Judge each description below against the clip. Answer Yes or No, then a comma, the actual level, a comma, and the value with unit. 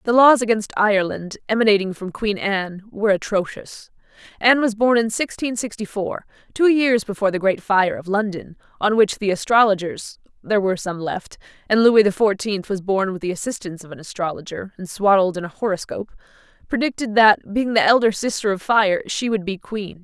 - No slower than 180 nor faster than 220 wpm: Yes, average, 185 wpm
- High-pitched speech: Yes, high, 205 Hz